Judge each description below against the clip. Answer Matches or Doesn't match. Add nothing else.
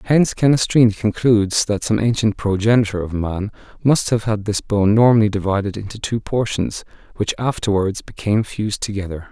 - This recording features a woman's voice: Doesn't match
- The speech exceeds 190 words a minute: Doesn't match